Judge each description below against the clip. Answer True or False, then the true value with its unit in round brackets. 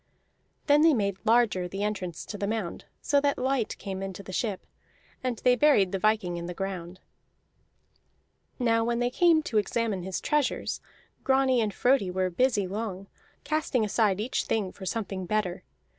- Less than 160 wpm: False (170 wpm)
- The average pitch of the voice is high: True (215 Hz)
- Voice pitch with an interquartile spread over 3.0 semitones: True (4.6 semitones)